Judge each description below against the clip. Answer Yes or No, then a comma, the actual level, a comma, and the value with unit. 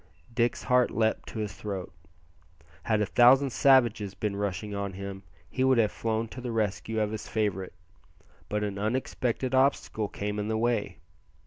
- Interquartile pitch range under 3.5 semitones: Yes, average, 2.8 semitones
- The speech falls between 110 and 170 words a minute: Yes, average, 165 wpm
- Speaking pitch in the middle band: No, low, 110 Hz